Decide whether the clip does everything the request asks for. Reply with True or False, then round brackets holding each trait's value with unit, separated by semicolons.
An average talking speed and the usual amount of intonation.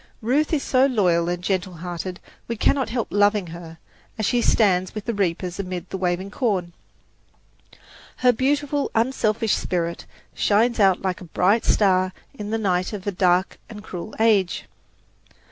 True (160 wpm; 3.9 semitones)